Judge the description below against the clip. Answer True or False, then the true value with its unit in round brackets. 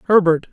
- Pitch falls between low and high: True (180 Hz)